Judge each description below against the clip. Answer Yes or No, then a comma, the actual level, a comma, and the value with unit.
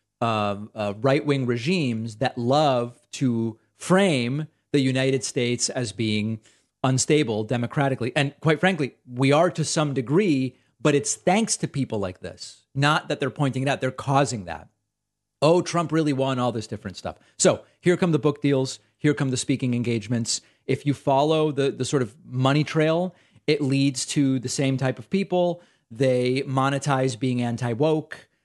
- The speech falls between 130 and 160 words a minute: No, average, 170 wpm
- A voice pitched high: No, low, 135 Hz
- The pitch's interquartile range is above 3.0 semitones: Yes, average, 3.6 semitones